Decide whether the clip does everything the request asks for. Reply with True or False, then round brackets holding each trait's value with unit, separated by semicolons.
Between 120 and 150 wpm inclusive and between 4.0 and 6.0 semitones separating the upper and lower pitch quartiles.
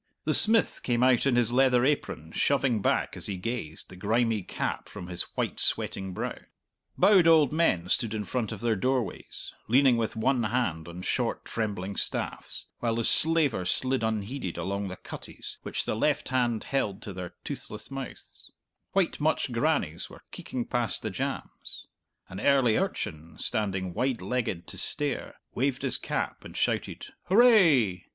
False (165 wpm; 5.6 semitones)